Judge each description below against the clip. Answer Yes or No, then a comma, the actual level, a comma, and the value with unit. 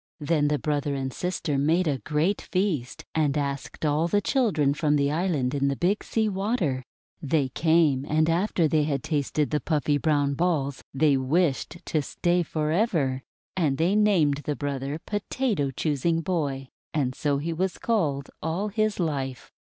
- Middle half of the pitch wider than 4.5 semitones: No, average, 3.8 semitones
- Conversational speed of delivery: Yes, average, 170 wpm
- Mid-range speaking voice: Yes, medium, 150 Hz